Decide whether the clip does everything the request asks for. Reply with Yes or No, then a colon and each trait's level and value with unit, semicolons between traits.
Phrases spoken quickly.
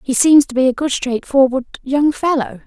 Yes: fast, 225 wpm